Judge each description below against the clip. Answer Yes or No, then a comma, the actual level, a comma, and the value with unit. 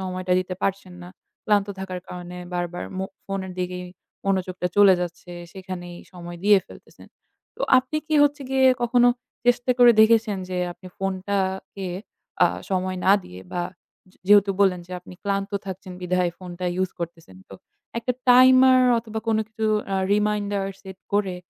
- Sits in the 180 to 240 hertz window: Yes, high, 190 Hz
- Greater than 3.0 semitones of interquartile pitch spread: No, narrow, 2.6 semitones